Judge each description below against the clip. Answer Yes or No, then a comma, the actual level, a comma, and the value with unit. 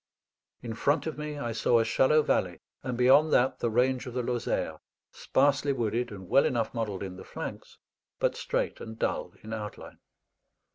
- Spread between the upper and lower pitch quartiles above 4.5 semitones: No, average, 3.4 semitones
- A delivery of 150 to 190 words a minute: Yes, average, 180 wpm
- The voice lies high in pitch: No, low, 125 Hz